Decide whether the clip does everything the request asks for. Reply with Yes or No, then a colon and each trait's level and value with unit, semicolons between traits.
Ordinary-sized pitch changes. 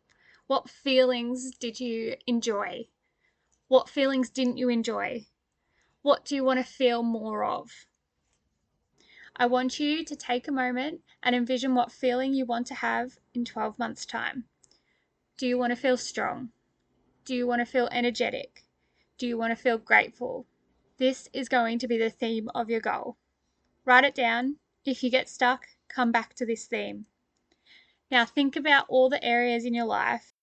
No: narrow, 1.6 semitones